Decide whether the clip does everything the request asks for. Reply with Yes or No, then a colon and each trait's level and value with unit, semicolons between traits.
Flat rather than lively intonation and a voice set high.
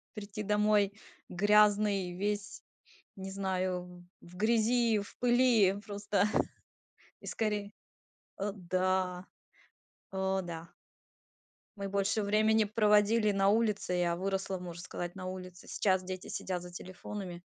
Yes: narrow, 2.3 semitones; high, 195 Hz